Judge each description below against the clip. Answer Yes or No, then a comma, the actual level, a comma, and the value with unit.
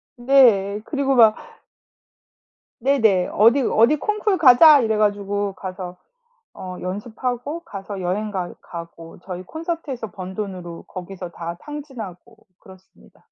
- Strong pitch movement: Yes, wide, 6.1 semitones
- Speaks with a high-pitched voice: Yes, high, 210 Hz